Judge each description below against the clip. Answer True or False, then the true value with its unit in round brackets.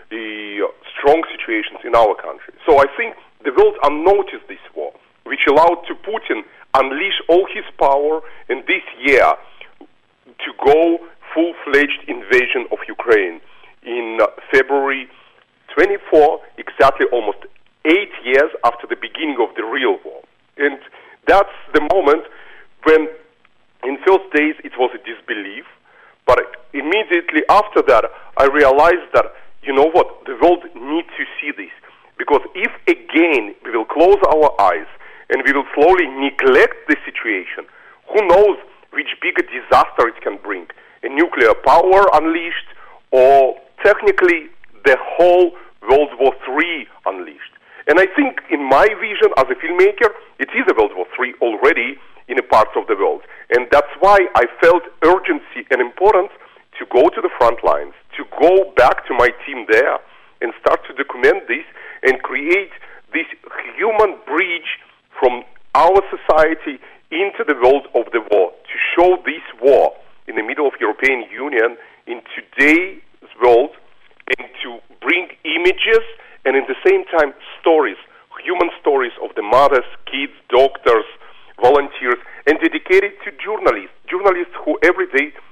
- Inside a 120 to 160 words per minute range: True (150 wpm)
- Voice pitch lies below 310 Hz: False (380 Hz)